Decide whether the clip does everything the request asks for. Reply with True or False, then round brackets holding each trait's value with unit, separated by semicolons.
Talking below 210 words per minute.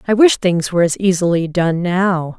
True (200 wpm)